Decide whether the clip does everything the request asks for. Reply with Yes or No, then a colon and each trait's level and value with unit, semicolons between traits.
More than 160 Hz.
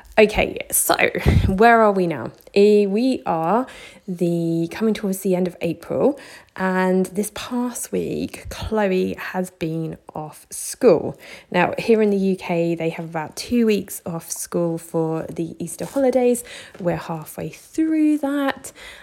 Yes: high, 190 Hz